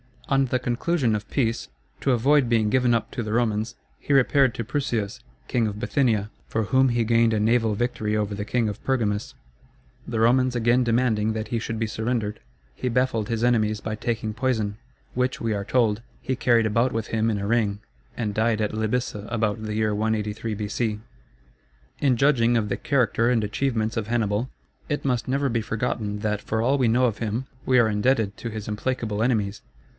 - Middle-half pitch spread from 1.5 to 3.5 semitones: Yes, narrow, 2.5 semitones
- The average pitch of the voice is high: No, low, 115 Hz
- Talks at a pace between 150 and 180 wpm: No, average, 195 wpm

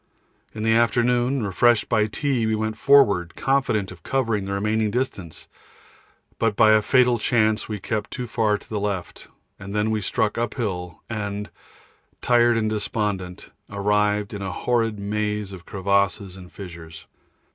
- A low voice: Yes, low, 105 Hz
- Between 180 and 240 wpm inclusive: No, average, 155 wpm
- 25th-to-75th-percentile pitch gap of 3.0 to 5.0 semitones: No, narrow, 2.6 semitones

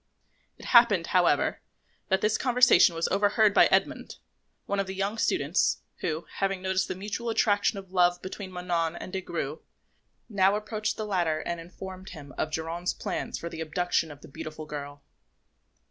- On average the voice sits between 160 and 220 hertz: Yes, medium, 185 Hz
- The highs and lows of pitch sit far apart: No, average, 3.6 semitones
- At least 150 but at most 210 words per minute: Yes, average, 170 wpm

